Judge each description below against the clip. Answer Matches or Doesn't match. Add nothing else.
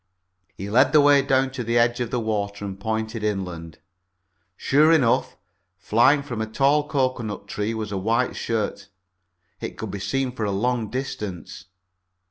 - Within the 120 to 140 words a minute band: Doesn't match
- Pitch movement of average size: Matches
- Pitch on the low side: Matches